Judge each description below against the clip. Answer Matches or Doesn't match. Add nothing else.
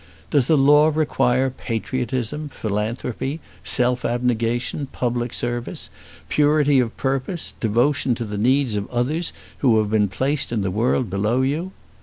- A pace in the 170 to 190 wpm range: Doesn't match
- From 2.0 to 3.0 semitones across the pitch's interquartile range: Doesn't match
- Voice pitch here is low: Matches